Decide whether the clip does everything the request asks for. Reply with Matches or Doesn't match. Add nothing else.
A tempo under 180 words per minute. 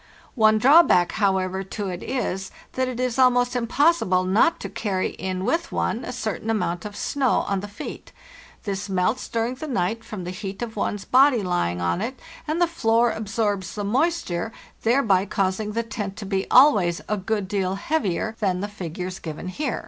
Doesn't match